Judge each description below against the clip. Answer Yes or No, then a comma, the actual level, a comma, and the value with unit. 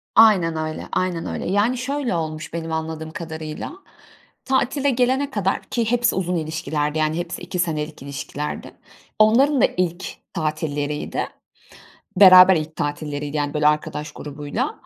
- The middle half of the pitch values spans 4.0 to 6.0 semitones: Yes, average, 5.2 semitones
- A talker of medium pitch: Yes, medium, 165 Hz